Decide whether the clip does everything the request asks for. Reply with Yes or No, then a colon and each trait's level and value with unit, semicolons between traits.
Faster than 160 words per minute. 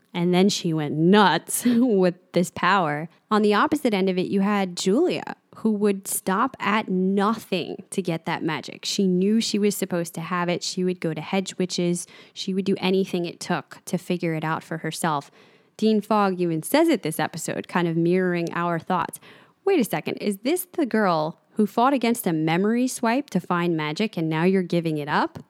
Yes: average, 200 wpm